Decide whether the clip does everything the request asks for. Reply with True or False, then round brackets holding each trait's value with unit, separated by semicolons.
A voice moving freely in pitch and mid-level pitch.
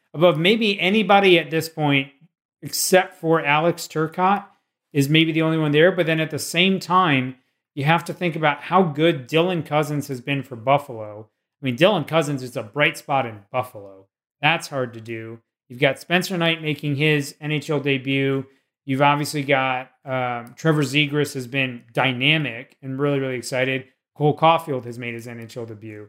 False (3.9 semitones; 145 Hz)